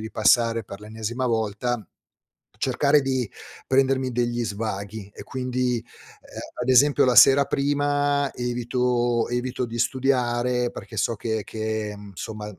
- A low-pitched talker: Yes, low, 120 Hz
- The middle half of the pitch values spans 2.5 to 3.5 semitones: Yes, average, 2.8 semitones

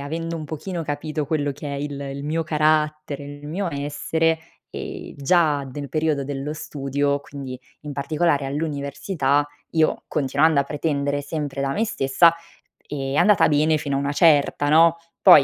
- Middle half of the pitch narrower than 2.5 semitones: Yes, narrow, 2.0 semitones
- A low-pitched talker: No, medium, 145 Hz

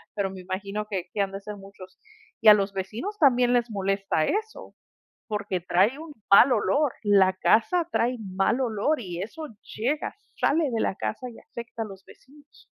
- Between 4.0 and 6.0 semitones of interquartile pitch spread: Yes, average, 4.6 semitones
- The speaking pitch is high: Yes, high, 210 Hz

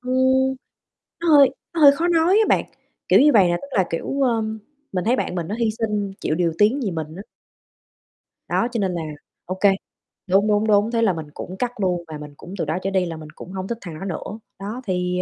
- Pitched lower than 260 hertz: Yes, high, 200 Hz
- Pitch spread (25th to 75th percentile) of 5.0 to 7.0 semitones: Yes, wide, 5.6 semitones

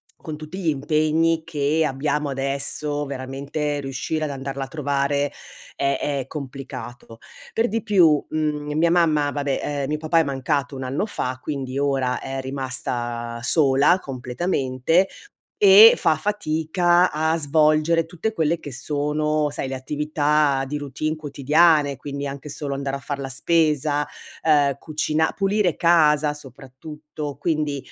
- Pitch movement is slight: Yes, narrow, 2.3 semitones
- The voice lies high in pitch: No, medium, 150 Hz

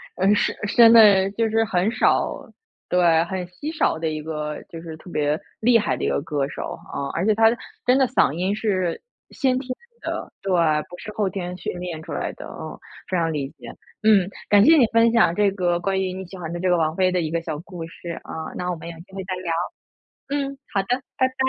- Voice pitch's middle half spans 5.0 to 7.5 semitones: No, average, 4.5 semitones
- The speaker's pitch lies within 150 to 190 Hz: Yes, medium, 185 Hz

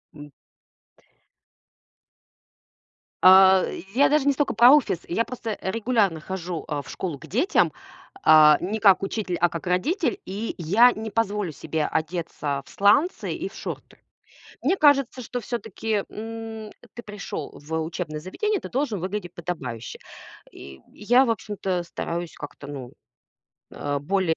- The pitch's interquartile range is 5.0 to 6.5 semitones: Yes, wide, 5.4 semitones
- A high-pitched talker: Yes, high, 195 Hz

